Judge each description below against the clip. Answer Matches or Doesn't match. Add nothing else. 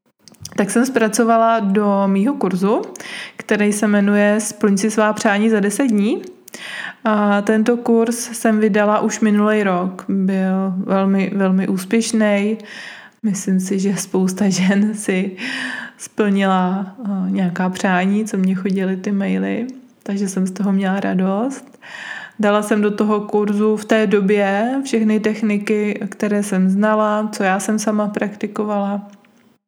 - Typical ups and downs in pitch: Doesn't match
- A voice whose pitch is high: Matches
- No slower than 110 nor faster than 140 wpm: Matches